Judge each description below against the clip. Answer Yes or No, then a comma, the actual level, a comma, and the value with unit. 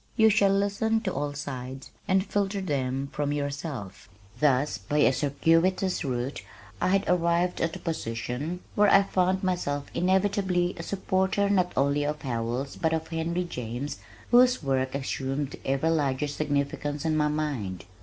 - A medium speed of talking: Yes, average, 155 wpm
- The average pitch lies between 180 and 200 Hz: No, medium, 150 Hz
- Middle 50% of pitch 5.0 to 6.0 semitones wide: Yes, average, 5.3 semitones